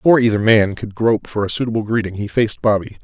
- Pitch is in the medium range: No, low, 110 Hz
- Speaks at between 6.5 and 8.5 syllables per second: Yes, 7.1 syllables/s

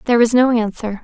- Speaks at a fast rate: Yes, fast, 230 wpm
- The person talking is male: No, female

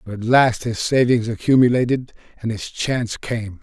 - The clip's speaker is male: Yes, male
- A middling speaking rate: Yes, average, 165 wpm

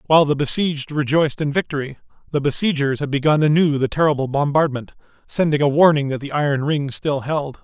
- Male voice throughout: Yes, male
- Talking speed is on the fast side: No, average, 180 wpm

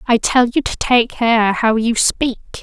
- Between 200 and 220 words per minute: Yes, fast, 205 wpm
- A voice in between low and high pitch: No, high, 235 Hz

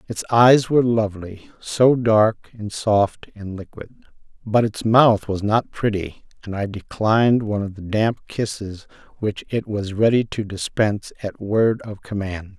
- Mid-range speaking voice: No, low, 105 Hz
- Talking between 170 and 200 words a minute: No, average, 160 wpm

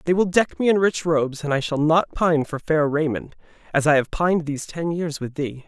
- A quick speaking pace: Yes, fast, 255 wpm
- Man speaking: Yes, male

